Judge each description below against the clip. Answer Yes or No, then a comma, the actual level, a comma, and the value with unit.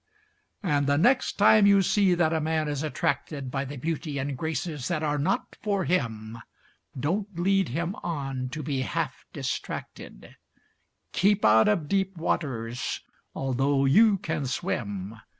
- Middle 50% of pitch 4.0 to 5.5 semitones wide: Yes, average, 5.2 semitones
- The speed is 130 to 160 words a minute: Yes, average, 150 wpm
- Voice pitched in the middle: Yes, medium, 150 Hz